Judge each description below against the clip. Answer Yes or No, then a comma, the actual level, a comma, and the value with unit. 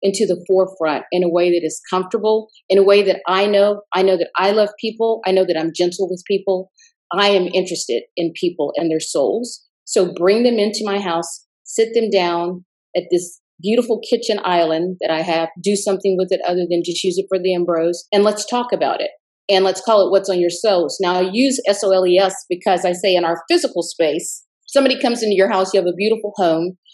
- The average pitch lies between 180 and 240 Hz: Yes, high, 190 Hz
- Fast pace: Yes, fast, 230 wpm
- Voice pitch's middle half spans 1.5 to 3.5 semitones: Yes, average, 2.8 semitones